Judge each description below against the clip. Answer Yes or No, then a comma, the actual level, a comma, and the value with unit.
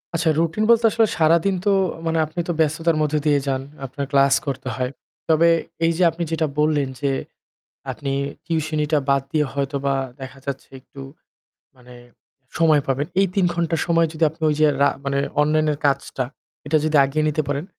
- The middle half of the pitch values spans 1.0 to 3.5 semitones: Yes, average, 2.9 semitones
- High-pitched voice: No, medium, 155 Hz